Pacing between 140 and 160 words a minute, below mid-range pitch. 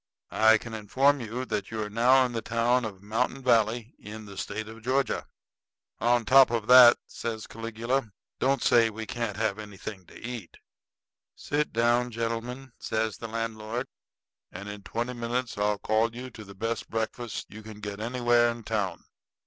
No: average, 175 wpm; low, 115 Hz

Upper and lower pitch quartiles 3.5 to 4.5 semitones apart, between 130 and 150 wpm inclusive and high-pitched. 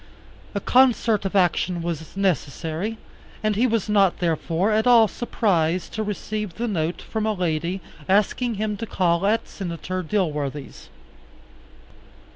Yes: average, 4.2 semitones; slow, 135 wpm; high, 195 Hz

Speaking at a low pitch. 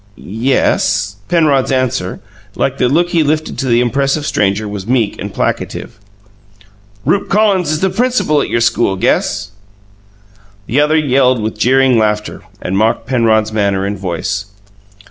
Yes: low, 125 Hz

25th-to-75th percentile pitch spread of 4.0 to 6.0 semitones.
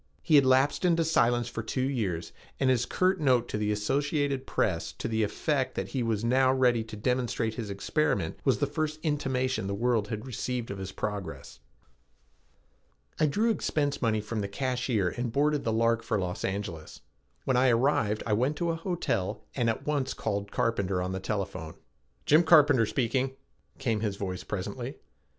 Yes: average, 4.6 semitones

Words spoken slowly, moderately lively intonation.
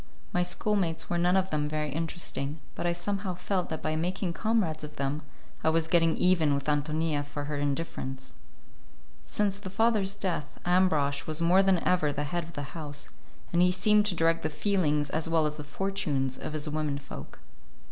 No: average, 190 wpm; average, 3.6 semitones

